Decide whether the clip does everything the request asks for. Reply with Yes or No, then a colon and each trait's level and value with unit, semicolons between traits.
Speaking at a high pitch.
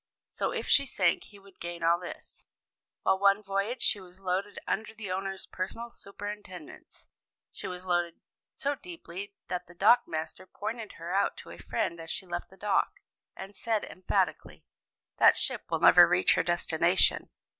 Yes: high, 195 Hz